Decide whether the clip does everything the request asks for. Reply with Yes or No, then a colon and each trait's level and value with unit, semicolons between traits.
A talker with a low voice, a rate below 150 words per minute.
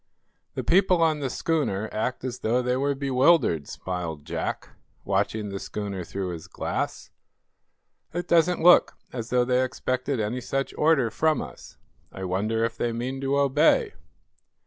No: low, 125 Hz; average, 155 wpm